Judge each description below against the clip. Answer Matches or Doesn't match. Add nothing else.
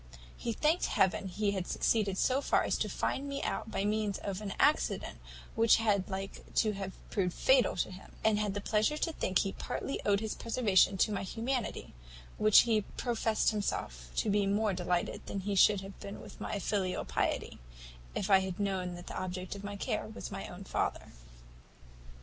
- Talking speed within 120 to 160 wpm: Doesn't match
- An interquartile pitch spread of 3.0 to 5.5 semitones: Doesn't match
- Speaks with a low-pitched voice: Doesn't match